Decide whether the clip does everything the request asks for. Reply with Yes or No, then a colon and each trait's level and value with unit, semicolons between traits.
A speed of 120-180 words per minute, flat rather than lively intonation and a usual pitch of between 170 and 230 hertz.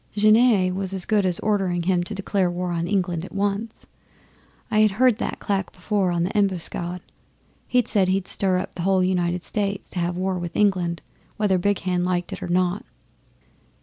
No: average, 190 wpm; narrow, 2.3 semitones; medium, 185 Hz